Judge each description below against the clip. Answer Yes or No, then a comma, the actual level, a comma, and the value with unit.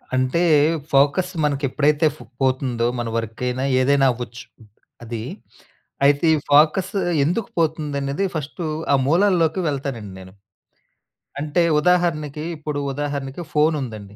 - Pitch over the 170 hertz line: No, medium, 145 Hz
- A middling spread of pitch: Yes, average, 3.2 semitones